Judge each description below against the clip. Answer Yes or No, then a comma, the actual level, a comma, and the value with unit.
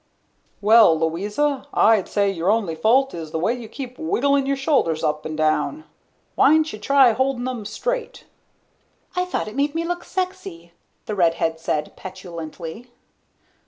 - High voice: Yes, high, 220 Hz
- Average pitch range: No, wide, 8.8 semitones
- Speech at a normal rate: Yes, average, 150 wpm